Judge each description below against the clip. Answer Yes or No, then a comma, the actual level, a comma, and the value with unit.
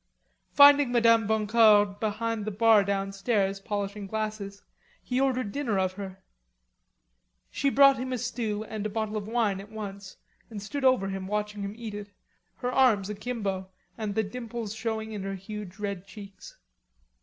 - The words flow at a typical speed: Yes, average, 160 wpm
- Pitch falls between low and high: No, high, 210 Hz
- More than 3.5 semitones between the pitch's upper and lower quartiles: No, narrow, 2.5 semitones